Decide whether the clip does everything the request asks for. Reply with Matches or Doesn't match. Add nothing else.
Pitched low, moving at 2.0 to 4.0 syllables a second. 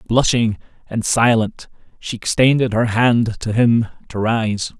Matches